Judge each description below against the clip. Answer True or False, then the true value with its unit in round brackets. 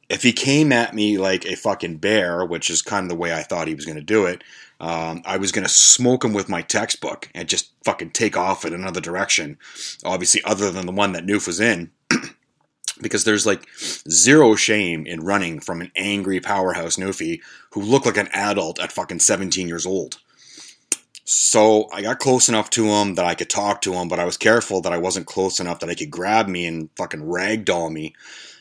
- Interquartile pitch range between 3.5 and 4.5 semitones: True (3.9 semitones)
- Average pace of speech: False (215 wpm)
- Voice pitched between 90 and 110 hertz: True (100 Hz)